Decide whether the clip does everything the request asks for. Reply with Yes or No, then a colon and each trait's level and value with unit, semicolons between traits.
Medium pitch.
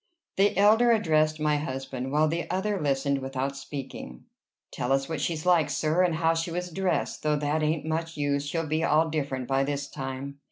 Yes: medium, 155 Hz